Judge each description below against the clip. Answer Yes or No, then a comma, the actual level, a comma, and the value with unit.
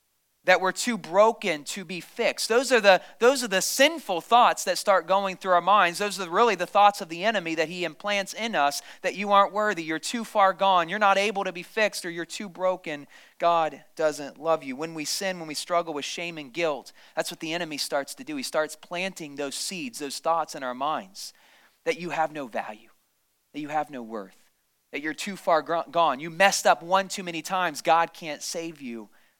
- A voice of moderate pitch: Yes, medium, 175 Hz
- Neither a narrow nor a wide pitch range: Yes, average, 3.9 semitones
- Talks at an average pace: No, fast, 220 wpm